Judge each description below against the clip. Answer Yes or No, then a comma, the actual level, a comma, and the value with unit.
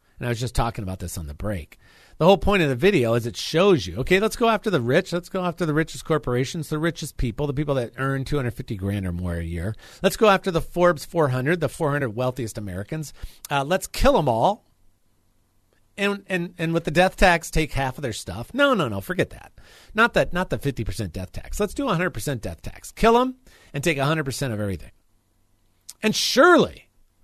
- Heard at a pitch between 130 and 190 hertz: Yes, low, 135 Hz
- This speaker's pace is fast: Yes, fast, 215 wpm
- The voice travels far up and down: Yes, wide, 8.7 semitones